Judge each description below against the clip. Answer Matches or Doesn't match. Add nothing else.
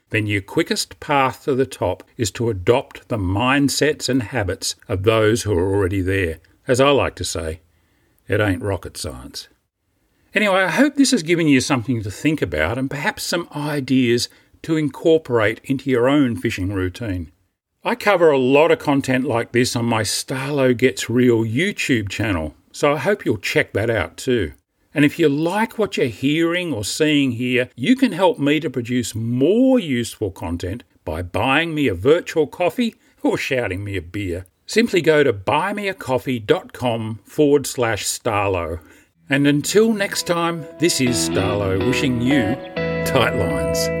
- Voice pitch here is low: Matches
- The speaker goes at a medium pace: Matches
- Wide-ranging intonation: Matches